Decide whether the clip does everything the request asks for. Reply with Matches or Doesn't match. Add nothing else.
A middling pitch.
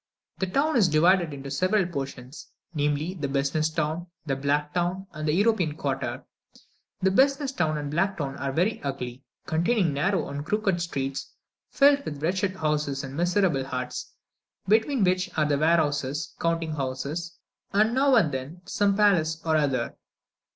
Matches